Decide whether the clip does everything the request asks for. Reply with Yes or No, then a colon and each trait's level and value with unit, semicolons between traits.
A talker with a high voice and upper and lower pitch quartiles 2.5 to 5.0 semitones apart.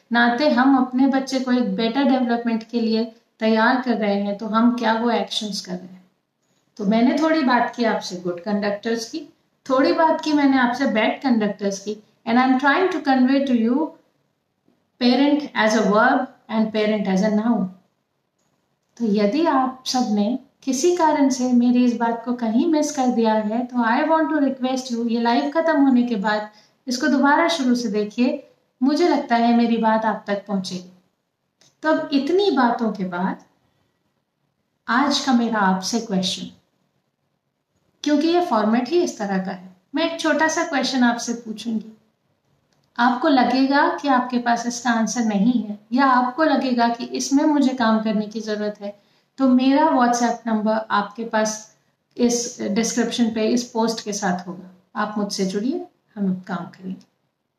Yes: high, 235 Hz; average, 3.8 semitones